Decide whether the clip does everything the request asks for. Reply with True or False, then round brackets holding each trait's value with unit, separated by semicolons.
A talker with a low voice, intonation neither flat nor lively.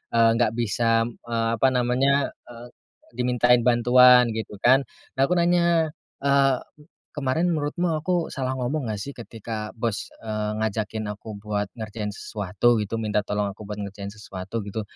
True (115 Hz; 3.7 semitones)